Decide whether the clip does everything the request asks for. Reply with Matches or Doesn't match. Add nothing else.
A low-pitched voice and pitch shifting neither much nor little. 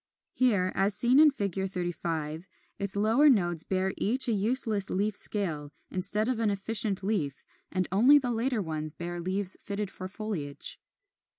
Doesn't match